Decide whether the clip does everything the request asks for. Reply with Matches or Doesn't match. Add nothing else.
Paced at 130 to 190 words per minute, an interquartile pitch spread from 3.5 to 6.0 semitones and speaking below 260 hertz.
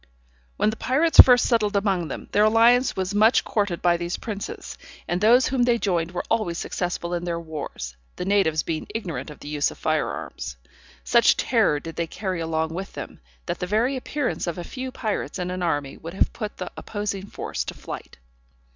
Doesn't match